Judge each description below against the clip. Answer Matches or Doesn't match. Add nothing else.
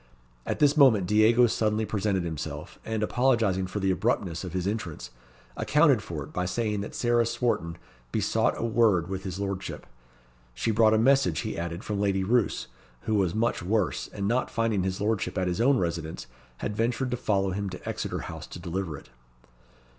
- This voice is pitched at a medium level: Doesn't match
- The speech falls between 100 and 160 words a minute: Doesn't match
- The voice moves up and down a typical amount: Matches